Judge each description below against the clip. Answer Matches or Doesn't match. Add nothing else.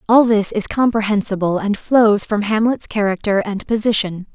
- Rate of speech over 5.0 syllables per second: Doesn't match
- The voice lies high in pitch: Matches